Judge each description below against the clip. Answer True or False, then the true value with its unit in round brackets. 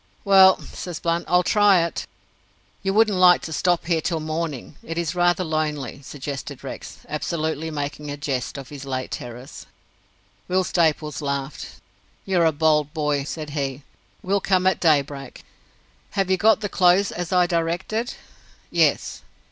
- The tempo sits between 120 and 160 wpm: True (155 wpm)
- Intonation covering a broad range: False (3.9 semitones)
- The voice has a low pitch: False (160 Hz)